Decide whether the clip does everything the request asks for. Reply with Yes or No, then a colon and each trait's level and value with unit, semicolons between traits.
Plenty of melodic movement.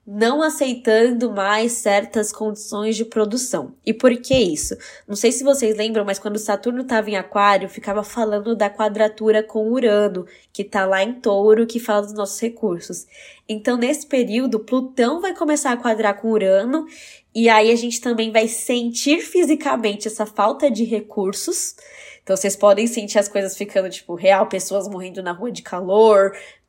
No: average, 2.9 semitones